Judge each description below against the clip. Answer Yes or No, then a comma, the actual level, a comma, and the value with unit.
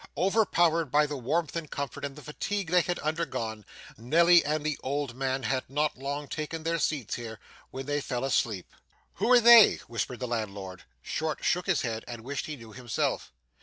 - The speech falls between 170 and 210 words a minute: Yes, average, 190 wpm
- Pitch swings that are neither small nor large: Yes, average, 5.0 semitones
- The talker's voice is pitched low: No, medium, 145 Hz